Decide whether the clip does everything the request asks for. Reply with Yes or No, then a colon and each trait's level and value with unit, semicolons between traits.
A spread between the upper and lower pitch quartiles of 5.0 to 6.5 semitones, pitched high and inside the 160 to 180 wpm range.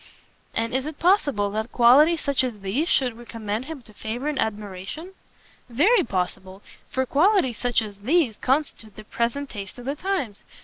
Yes: wide, 5.5 semitones; high, 245 Hz; average, 170 wpm